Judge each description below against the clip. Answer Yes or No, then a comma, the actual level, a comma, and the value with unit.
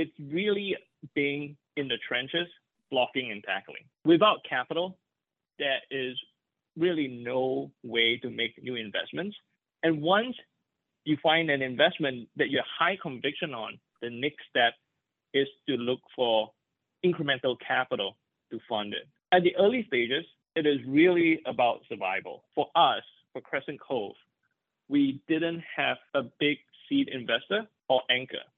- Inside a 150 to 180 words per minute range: No, average, 140 wpm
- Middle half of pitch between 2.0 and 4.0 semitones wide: No, wide, 5.4 semitones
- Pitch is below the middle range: No, medium, 145 Hz